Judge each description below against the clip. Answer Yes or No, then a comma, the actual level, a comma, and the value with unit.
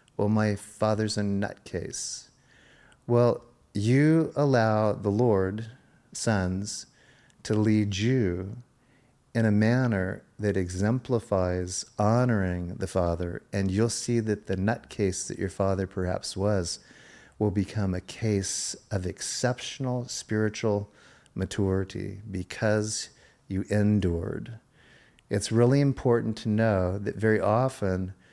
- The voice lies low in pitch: Yes, low, 105 Hz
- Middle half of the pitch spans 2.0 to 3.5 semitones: Yes, average, 3.0 semitones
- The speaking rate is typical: No, slow, 110 wpm